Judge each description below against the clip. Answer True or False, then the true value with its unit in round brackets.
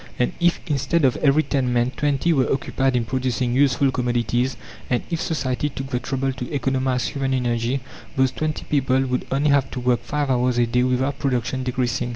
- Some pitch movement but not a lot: False (1.8 semitones)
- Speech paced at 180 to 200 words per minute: True (190 wpm)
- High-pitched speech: False (130 Hz)